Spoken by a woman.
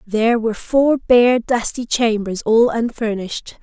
Yes: female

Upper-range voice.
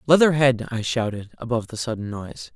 No: low, 120 Hz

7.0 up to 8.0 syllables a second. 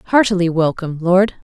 No: 5.5 syllables/s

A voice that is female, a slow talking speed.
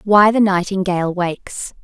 Yes: female; slow, 130 wpm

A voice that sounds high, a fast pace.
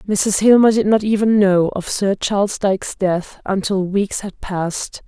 No: high, 200 Hz; average, 180 wpm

